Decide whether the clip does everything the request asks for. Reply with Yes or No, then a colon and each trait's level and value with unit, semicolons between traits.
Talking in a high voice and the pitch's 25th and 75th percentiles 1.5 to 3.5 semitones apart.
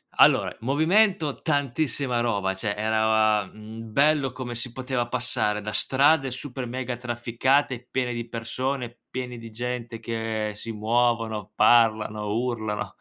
No: low, 120 Hz; average, 2.8 semitones